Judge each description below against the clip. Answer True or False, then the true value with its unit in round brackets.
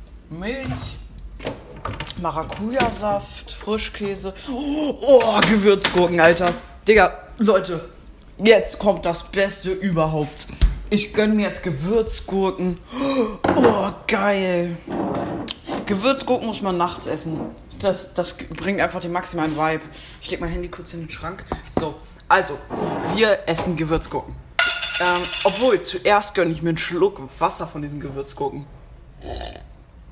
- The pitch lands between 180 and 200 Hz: True (185 Hz)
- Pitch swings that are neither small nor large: True (3.8 semitones)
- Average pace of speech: False (115 wpm)